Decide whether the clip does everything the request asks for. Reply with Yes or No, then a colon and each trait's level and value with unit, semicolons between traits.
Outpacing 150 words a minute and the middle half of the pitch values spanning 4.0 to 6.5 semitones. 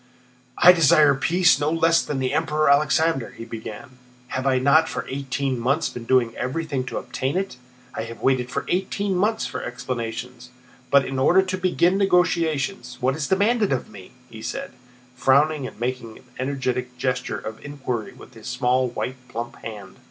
Yes: average, 170 wpm; average, 4.4 semitones